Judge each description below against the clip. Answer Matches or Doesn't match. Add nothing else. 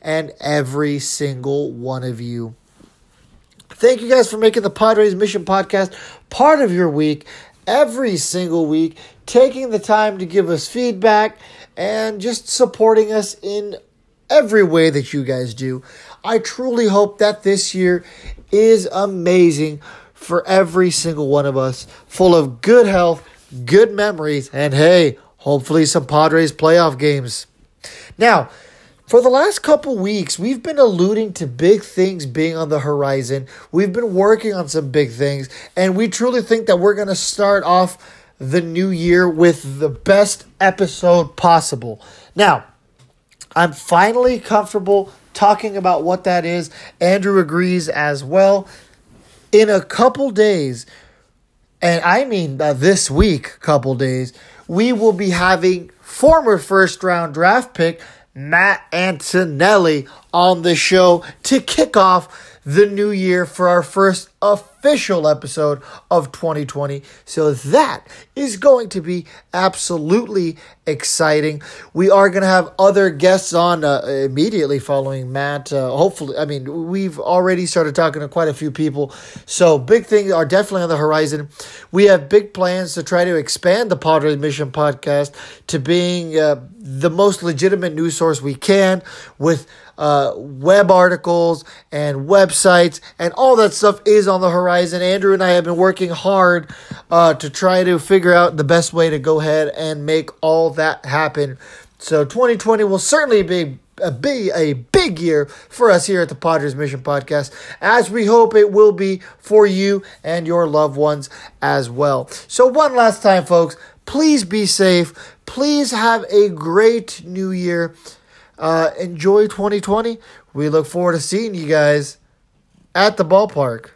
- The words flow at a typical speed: Matches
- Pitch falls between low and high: Matches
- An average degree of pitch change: Matches